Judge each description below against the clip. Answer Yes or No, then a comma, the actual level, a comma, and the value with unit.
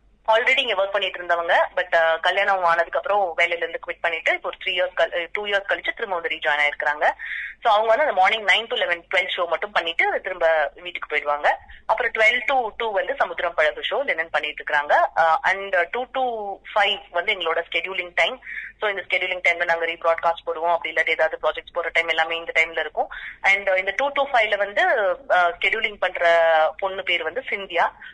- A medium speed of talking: No, fast, 185 wpm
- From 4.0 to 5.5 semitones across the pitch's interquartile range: No, average, 3.5 semitones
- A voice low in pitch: No, medium, 175 Hz